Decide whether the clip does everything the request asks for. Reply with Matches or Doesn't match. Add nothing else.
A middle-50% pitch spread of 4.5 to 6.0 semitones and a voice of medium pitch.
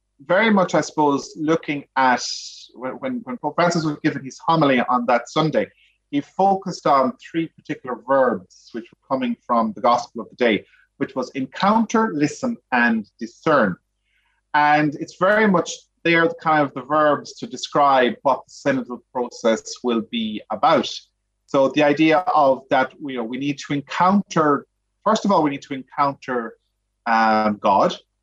Matches